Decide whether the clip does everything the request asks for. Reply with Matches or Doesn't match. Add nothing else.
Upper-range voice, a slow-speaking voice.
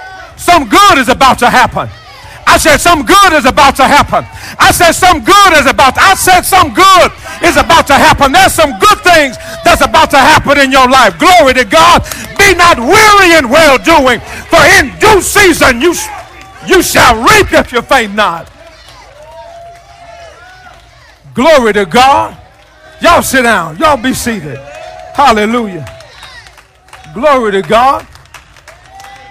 Doesn't match